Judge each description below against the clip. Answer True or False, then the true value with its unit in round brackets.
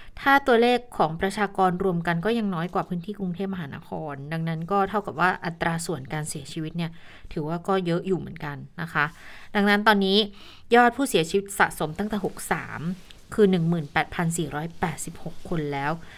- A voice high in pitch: False (180 Hz)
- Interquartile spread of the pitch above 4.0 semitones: False (3.5 semitones)